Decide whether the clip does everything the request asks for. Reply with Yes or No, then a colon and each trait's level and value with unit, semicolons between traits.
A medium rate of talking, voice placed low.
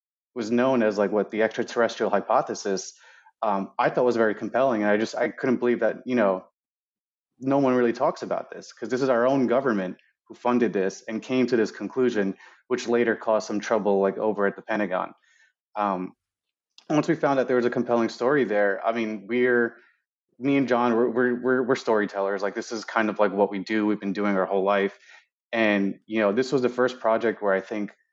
No: fast, 220 wpm; low, 110 Hz